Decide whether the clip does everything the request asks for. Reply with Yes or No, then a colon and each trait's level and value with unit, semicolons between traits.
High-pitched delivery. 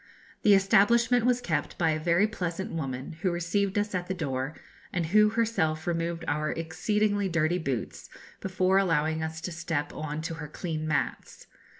No: medium, 170 Hz